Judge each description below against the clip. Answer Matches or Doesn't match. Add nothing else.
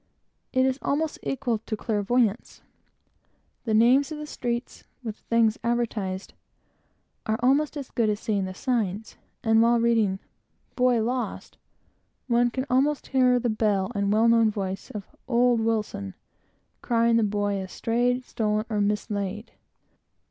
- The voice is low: Doesn't match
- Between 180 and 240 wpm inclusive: Doesn't match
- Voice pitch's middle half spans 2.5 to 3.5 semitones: Matches